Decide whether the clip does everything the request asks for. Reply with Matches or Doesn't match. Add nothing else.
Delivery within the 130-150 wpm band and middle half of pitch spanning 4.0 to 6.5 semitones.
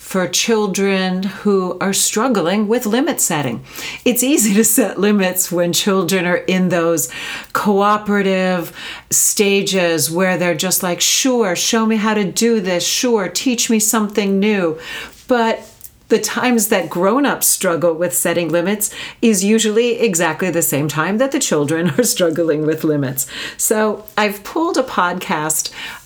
Matches